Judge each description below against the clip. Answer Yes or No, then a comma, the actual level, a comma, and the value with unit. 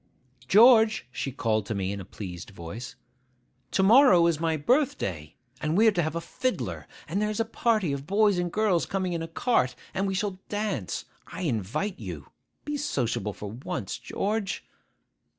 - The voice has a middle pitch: Yes, medium, 170 Hz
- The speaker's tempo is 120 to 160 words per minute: No, average, 175 wpm